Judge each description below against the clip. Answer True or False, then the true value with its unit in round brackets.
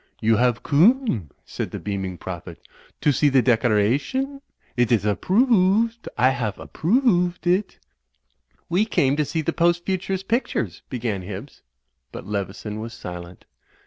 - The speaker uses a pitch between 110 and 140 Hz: True (135 Hz)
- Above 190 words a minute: False (150 wpm)